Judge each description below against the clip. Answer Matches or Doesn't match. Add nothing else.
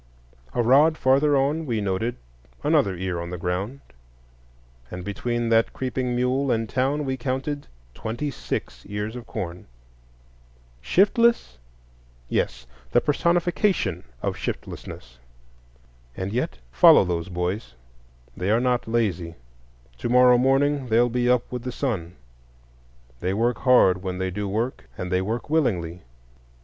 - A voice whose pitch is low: Matches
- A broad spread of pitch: Matches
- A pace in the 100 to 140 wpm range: Matches